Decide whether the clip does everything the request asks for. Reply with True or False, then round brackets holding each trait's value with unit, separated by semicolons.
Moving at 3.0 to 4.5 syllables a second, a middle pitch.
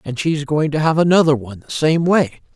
False (5.6 syllables/s; 150 Hz)